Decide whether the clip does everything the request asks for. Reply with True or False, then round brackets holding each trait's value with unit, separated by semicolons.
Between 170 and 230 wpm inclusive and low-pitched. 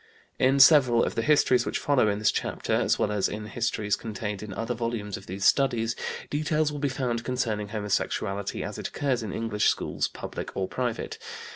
True (190 wpm; 115 Hz)